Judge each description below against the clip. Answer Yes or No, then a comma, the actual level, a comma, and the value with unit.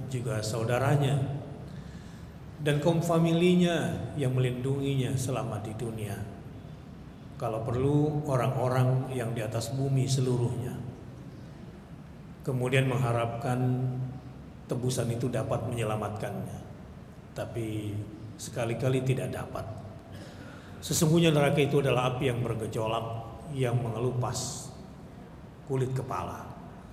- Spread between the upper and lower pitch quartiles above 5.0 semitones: No, average, 2.8 semitones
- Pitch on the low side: Yes, low, 130 Hz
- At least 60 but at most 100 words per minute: Yes, slow, 85 wpm